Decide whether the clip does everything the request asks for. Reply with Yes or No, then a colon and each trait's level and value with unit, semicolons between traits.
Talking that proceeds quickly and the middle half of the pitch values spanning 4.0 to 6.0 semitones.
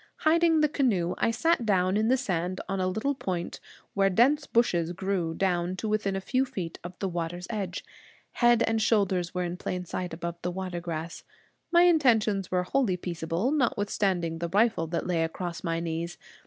No: average, 185 wpm; average, 4.7 semitones